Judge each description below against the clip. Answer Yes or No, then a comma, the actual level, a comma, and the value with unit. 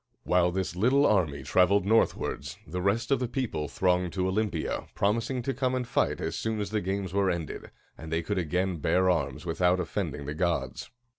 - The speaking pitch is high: No, very low, 95 Hz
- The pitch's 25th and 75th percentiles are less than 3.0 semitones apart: No, average, 3.8 semitones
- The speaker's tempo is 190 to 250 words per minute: Yes, average, 195 wpm